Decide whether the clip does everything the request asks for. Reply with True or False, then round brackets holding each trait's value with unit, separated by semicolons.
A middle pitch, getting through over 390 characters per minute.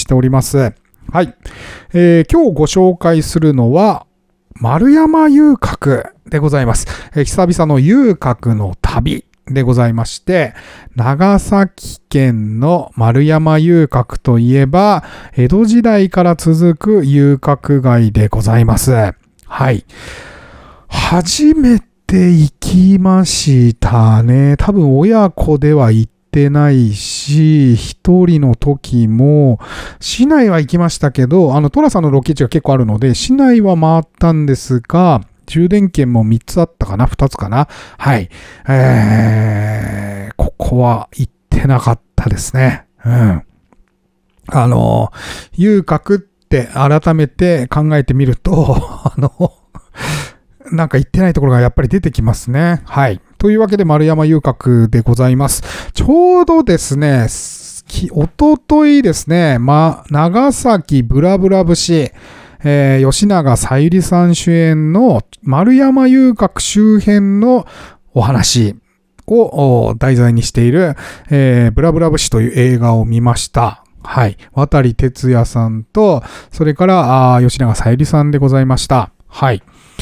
False (145 Hz; 245 characters per minute)